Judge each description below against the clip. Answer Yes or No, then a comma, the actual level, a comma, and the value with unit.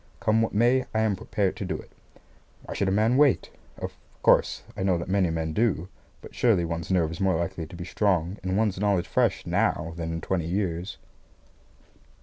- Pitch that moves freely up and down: No, average, 3.8 semitones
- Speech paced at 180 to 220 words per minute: Yes, average, 200 wpm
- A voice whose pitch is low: Yes, very low, 95 Hz